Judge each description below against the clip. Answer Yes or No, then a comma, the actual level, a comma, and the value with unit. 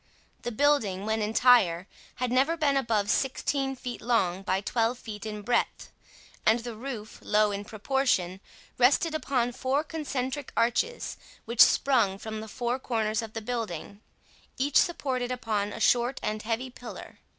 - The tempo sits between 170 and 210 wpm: No, average, 150 wpm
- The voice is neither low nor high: No, high, 235 Hz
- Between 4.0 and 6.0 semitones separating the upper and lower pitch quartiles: No, average, 3.5 semitones